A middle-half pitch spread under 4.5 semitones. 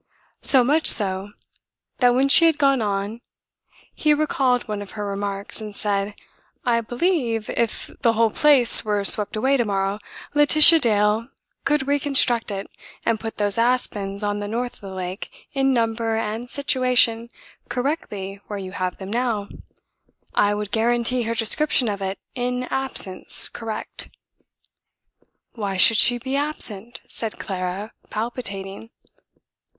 Yes: average, 3.6 semitones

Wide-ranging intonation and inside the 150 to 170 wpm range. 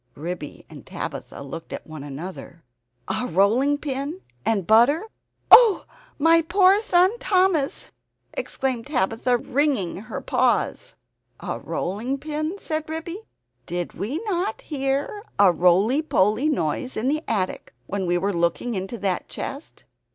No: wide, 8.8 semitones; slow, 135 wpm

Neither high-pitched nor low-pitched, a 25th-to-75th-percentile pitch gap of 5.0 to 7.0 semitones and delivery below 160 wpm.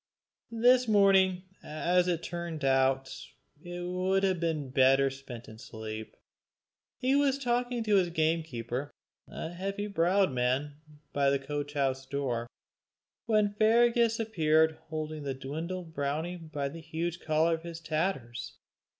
Yes: medium, 160 Hz; wide, 5.4 semitones; slow, 135 wpm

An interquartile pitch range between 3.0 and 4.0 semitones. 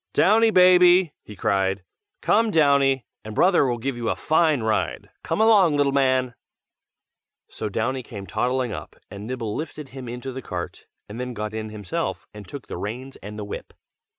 No: wide, 5.5 semitones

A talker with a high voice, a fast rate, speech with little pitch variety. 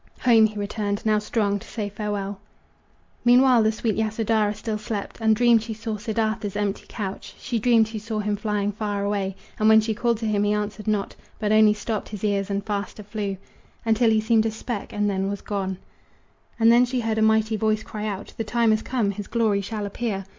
Yes: high, 215 Hz; fast, 210 wpm; narrow, 1.5 semitones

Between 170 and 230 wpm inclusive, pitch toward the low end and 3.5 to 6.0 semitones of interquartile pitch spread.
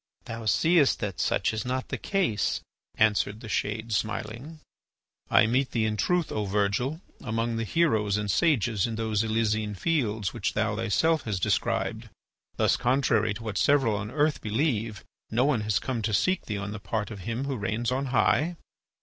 Yes: average, 180 wpm; low, 110 Hz; average, 3.8 semitones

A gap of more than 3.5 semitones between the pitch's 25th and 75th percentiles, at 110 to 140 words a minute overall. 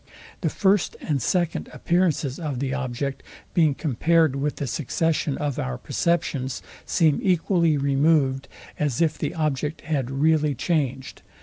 No: average, 3.2 semitones; slow, 135 wpm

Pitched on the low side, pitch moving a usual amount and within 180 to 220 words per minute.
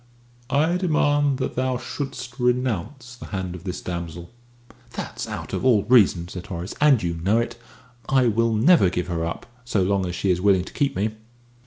No: low, 110 Hz; wide, 6.3 semitones; average, 190 wpm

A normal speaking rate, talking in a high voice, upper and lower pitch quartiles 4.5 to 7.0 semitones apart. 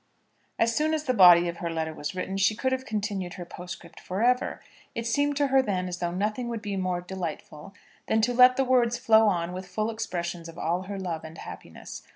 No: fast, 225 wpm; high, 195 Hz; average, 4.9 semitones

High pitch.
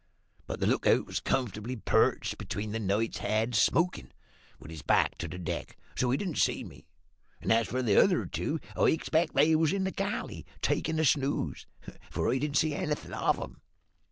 No: low, 130 Hz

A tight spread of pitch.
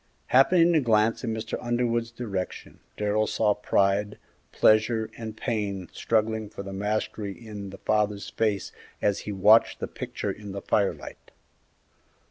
Yes: narrow, 1.9 semitones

